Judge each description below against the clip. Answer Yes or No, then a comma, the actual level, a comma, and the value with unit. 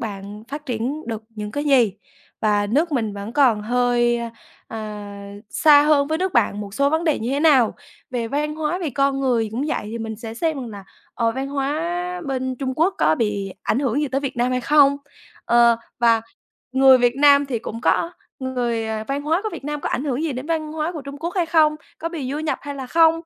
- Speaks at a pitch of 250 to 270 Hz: Yes, very high, 265 Hz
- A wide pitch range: No, average, 4.8 semitones